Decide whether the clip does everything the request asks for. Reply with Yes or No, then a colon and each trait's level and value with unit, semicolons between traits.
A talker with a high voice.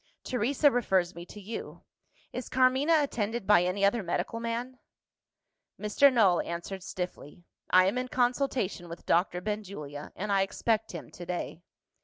Yes: high, 205 Hz